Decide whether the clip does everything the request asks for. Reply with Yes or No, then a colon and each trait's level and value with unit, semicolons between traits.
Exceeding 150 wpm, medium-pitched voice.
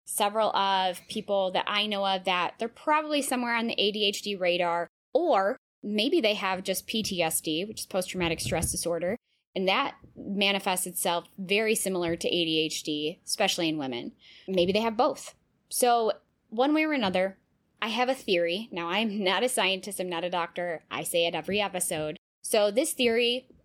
No: average, 175 wpm; high, 195 Hz